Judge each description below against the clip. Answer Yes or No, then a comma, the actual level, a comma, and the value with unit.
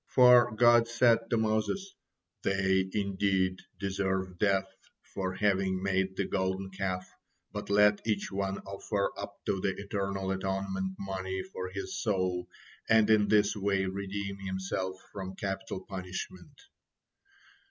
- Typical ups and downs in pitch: No, narrow, 1.4 semitones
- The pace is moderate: No, slow, 130 wpm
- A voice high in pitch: No, very low, 95 Hz